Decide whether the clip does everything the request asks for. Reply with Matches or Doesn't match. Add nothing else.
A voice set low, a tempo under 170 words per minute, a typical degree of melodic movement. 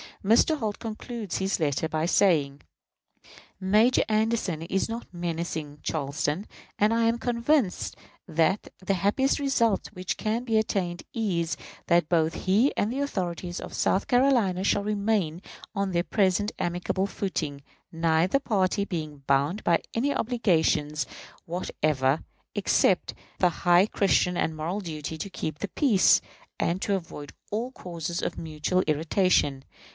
Doesn't match